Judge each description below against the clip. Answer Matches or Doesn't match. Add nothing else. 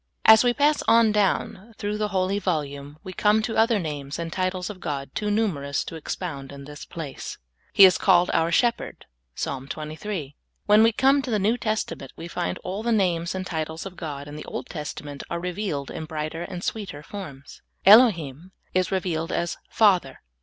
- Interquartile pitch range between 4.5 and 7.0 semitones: Matches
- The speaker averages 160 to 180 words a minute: Doesn't match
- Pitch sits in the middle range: Matches